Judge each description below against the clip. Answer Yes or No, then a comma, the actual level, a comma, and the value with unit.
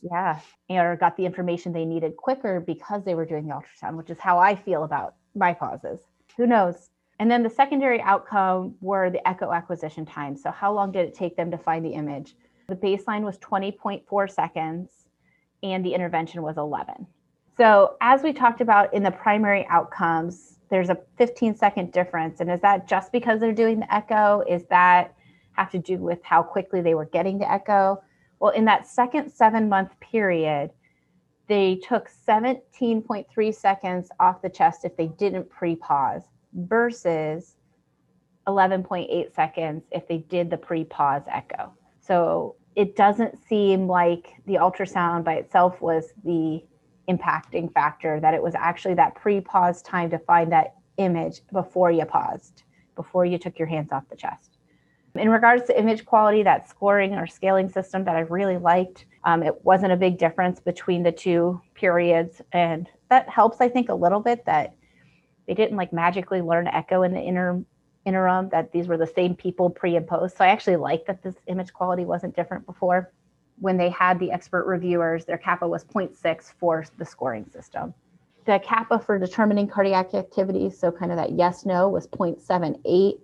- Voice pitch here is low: No, medium, 185 Hz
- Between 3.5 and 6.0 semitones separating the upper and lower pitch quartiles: No, average, 2.9 semitones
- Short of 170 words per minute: No, average, 180 wpm